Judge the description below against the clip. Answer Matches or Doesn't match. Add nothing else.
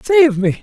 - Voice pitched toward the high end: Matches